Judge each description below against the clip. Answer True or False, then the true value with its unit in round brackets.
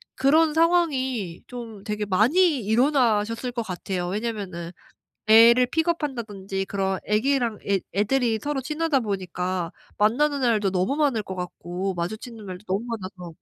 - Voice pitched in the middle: False (220 Hz)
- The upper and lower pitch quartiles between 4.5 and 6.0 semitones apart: True (5.5 semitones)